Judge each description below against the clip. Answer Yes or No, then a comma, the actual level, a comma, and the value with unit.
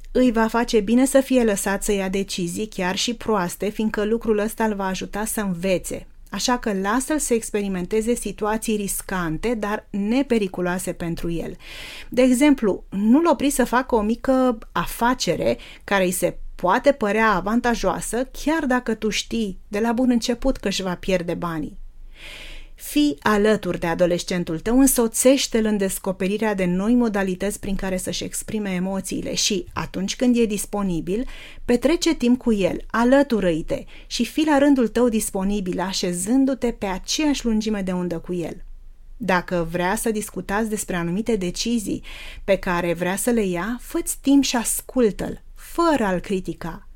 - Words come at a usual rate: Yes, average, 155 wpm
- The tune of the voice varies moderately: Yes, average, 4.5 semitones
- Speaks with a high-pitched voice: Yes, high, 215 Hz